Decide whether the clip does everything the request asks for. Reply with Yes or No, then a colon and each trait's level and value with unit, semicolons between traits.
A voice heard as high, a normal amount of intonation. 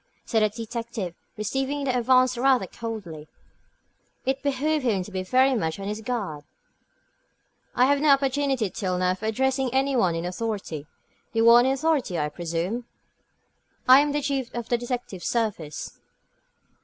No: high, 235 Hz; wide, 5.7 semitones